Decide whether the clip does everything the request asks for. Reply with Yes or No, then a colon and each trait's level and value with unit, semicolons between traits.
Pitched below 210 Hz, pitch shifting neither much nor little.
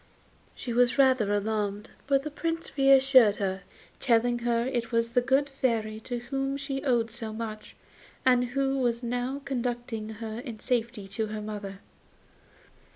No: high, 240 Hz; average, 3.4 semitones